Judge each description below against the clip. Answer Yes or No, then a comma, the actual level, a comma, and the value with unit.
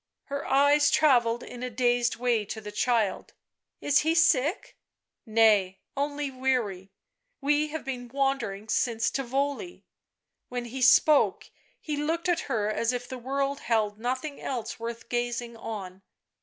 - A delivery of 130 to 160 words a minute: Yes, average, 155 wpm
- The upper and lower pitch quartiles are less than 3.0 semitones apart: No, average, 3.6 semitones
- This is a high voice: Yes, very high, 250 Hz